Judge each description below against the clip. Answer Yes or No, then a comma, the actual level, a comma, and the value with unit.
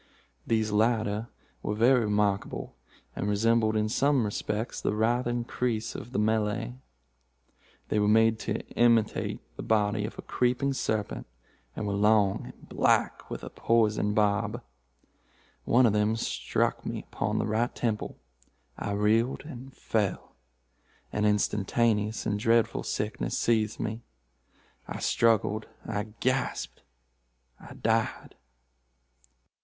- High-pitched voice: No, low, 110 Hz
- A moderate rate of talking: No, slow, 120 wpm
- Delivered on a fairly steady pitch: Yes, narrow, 1.9 semitones